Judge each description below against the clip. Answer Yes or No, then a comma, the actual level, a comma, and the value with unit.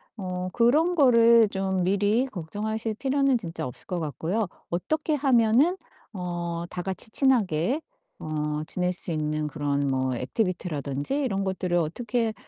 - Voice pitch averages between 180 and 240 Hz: Yes, high, 190 Hz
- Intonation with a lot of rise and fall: Yes, wide, 6.2 semitones